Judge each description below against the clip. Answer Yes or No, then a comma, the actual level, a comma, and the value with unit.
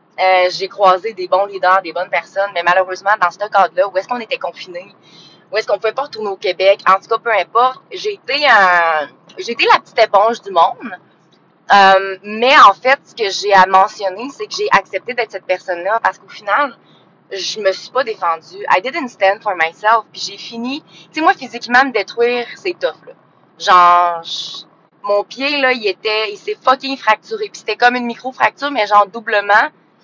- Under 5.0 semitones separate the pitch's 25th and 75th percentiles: No, wide, 5.4 semitones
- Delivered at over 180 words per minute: Yes, average, 205 wpm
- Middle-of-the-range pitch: No, high, 205 Hz